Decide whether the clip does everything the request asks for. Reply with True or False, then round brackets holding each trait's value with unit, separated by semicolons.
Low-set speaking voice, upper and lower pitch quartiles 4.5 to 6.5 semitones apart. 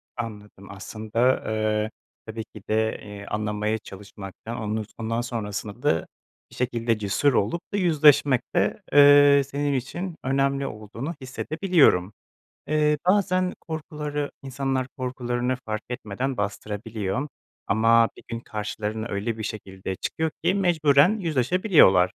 True (120 Hz; 5.1 semitones)